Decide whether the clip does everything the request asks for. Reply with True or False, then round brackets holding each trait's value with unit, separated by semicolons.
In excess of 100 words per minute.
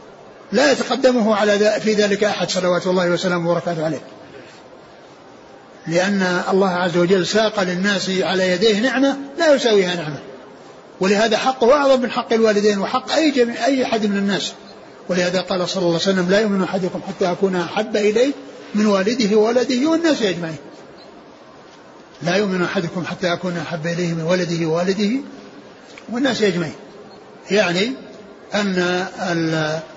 True (135 wpm)